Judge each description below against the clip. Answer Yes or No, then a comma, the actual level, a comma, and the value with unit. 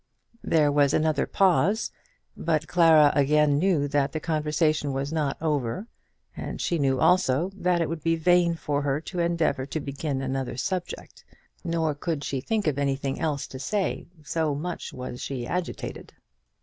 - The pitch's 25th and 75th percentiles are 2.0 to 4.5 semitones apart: Yes, average, 3.1 semitones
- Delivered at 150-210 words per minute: Yes, average, 160 wpm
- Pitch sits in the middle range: Yes, medium, 150 Hz